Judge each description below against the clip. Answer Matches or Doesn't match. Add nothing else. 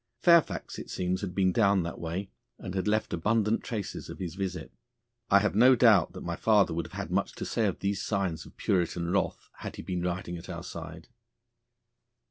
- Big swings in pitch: Doesn't match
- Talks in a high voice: Doesn't match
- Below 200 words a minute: Doesn't match